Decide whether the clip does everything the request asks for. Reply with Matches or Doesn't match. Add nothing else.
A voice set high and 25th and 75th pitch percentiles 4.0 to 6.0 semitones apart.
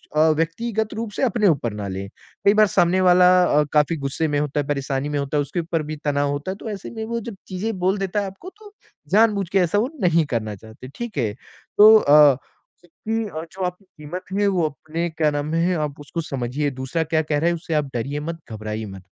Doesn't match